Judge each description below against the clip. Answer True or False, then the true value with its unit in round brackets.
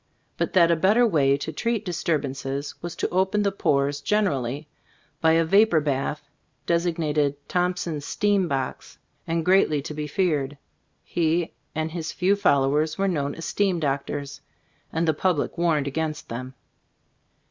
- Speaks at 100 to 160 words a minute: True (150 wpm)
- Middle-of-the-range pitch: True (160 Hz)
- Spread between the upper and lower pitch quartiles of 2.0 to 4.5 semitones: True (3.9 semitones)